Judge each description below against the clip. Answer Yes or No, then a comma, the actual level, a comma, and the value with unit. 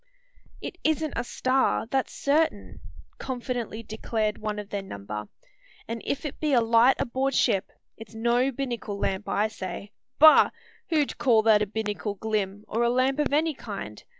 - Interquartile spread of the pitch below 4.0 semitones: No, average, 4.3 semitones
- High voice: Yes, high, 230 Hz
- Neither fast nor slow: Yes, average, 165 wpm